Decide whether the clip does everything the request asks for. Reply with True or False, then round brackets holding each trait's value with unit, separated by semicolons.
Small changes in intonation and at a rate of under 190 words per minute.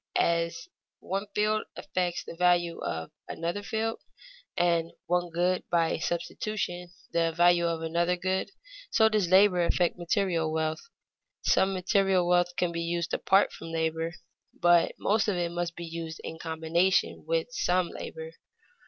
True (2.2 semitones; 145 wpm)